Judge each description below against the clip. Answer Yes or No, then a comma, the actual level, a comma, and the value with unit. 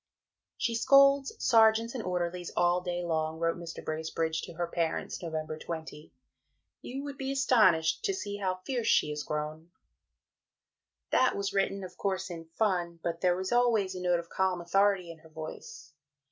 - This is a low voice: No, medium, 180 Hz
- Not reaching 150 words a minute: No, average, 170 wpm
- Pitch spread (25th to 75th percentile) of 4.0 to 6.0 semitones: Yes, average, 4.5 semitones